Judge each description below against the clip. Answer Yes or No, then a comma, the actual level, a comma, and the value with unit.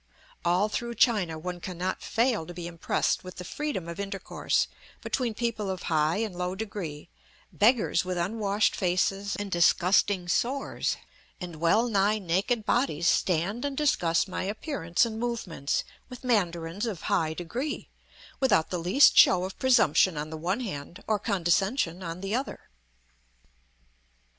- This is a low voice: No, high, 190 Hz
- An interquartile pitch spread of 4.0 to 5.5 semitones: Yes, average, 4.5 semitones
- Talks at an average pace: Yes, average, 150 wpm